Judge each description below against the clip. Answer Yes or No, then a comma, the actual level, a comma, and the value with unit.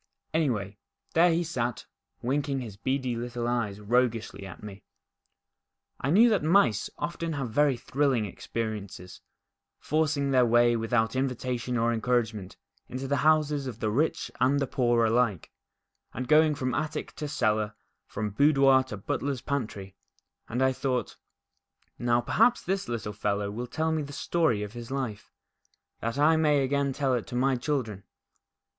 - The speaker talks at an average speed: Yes, average, 150 wpm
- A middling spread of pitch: Yes, average, 4.1 semitones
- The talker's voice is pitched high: No, low, 125 Hz